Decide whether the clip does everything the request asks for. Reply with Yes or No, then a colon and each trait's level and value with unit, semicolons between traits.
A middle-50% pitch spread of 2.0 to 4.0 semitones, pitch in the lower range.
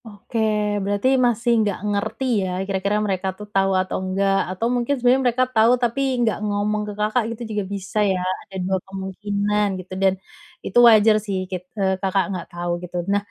No: narrow, 2.6 semitones; high, 200 Hz